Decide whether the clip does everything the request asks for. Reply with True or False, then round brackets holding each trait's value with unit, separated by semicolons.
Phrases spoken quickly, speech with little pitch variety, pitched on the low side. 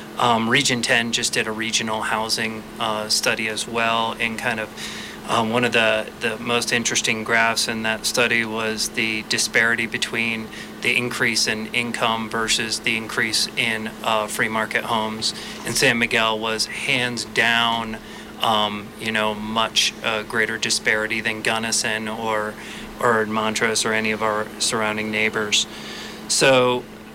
False (150 wpm; 1.1 semitones; 110 Hz)